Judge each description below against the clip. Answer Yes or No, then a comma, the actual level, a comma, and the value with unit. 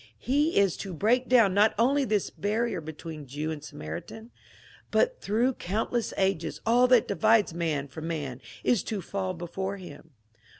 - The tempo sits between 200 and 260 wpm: No, average, 165 wpm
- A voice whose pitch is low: No, high, 195 Hz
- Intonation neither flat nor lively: No, wide, 6.1 semitones